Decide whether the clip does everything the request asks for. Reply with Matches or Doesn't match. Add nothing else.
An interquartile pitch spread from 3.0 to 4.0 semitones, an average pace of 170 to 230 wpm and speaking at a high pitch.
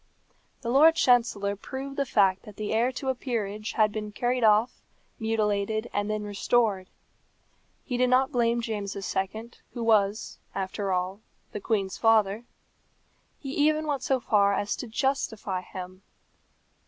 Doesn't match